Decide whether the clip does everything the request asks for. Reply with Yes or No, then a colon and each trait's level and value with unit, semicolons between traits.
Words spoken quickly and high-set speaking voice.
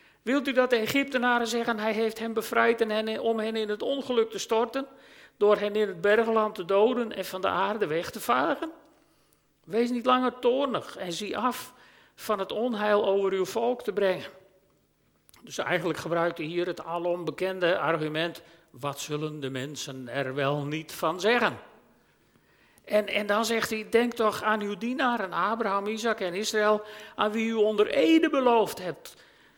No: average, 175 wpm; high, 210 Hz